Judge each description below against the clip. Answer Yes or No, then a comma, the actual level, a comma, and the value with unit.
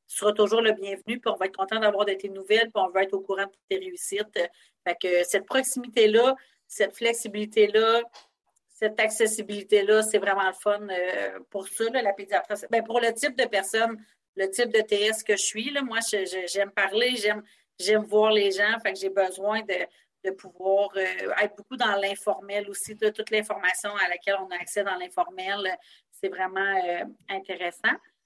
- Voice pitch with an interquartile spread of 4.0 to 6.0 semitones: No, narrow, 2.4 semitones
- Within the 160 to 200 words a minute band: Yes, average, 190 wpm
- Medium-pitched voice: No, high, 210 Hz